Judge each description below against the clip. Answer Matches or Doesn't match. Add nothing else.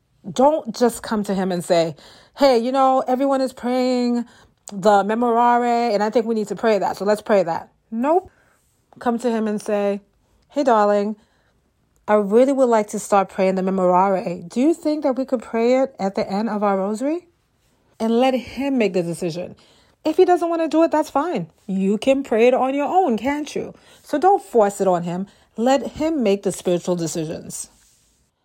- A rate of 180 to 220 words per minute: Matches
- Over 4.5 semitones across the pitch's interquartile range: Matches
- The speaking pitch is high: Matches